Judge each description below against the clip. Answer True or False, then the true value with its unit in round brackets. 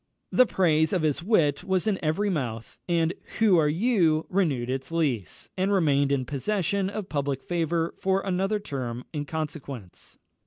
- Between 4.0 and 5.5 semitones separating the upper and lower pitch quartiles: True (5.2 semitones)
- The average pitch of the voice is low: False (160 Hz)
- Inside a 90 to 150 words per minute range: False (160 wpm)